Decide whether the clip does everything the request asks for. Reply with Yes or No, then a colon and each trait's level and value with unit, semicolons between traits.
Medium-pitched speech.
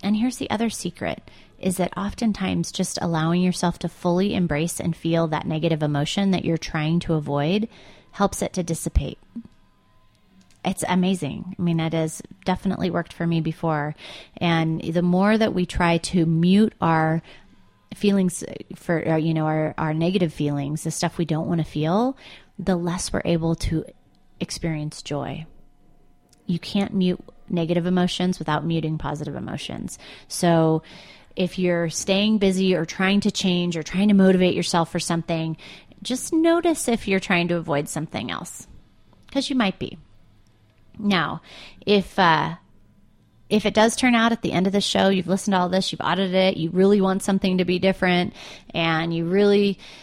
Yes: medium, 175 Hz